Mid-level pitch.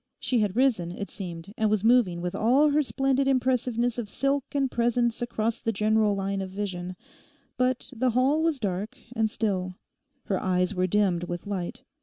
No: high, 220 Hz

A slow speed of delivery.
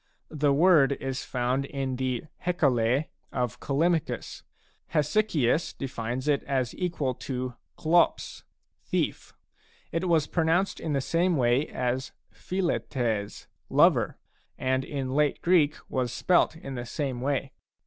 Yes: slow, 130 wpm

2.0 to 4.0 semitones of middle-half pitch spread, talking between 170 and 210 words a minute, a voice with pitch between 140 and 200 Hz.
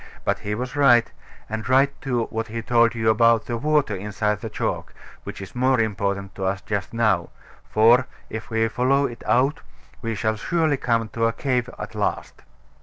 No: average, 2.7 semitones; average, 185 wpm; low, 115 Hz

